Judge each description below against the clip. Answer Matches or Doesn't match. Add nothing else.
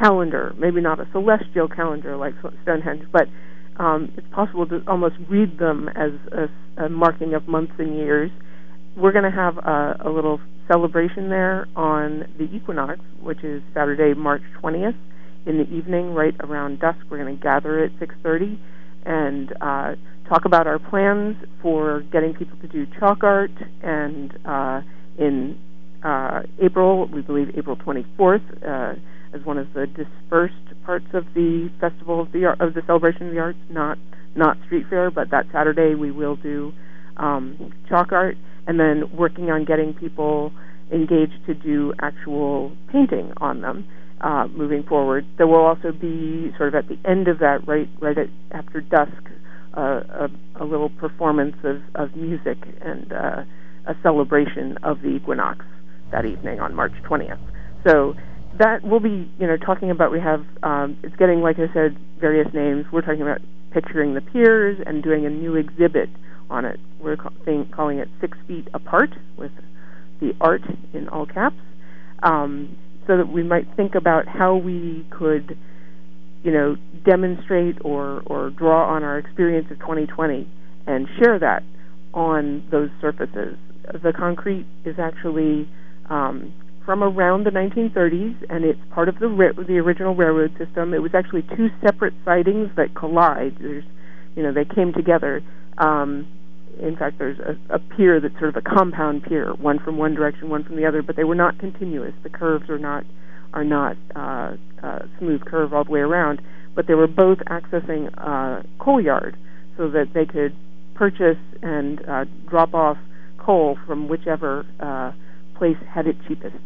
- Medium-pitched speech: Matches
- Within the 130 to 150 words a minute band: Doesn't match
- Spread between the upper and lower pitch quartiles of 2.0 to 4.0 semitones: Matches